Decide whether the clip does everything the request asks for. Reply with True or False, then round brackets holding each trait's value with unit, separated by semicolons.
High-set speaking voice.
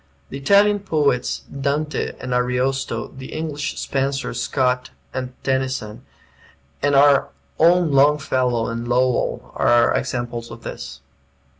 False (135 Hz)